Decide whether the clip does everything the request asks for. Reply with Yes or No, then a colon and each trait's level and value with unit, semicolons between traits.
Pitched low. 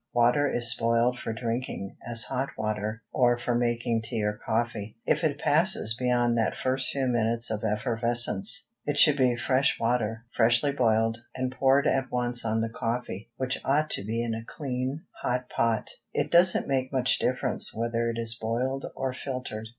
Yes: low, 120 Hz